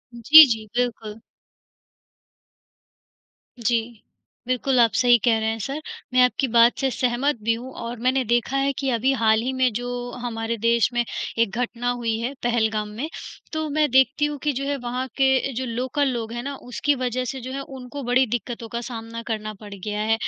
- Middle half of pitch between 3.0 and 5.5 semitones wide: No, narrow, 2.4 semitones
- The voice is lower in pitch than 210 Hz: No, high, 245 Hz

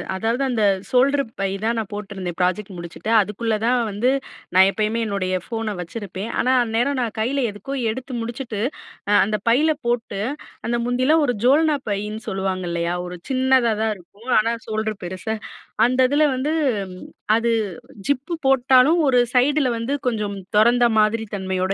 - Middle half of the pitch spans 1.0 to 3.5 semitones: No, average, 4.0 semitones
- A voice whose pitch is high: Yes, high, 225 Hz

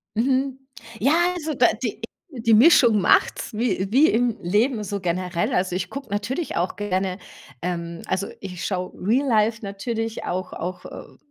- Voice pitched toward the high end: Yes, high, 210 Hz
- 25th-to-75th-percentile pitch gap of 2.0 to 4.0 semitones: No, average, 5.0 semitones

